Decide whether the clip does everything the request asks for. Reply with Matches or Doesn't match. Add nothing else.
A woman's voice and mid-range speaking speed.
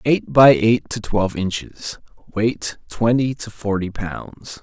Doesn't match